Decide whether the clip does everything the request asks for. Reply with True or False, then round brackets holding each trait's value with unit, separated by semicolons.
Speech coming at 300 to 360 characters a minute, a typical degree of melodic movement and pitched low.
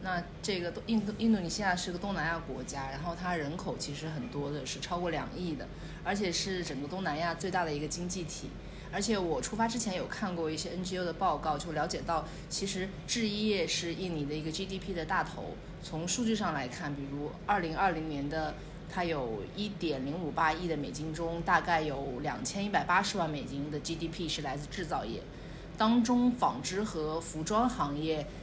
False (310 characters per minute; 3.5 semitones; 170 Hz)